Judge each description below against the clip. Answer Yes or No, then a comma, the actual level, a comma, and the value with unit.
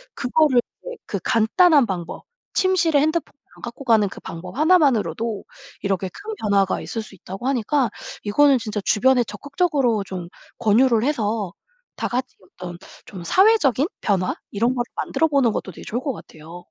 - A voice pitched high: Yes, high, 235 Hz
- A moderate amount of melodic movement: No, wide, 6.1 semitones